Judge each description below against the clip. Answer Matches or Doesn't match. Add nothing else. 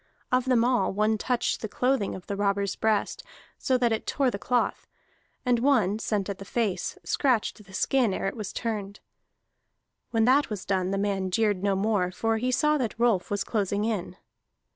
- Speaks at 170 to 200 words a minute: Matches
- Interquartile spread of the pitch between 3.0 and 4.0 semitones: Matches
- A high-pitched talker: Matches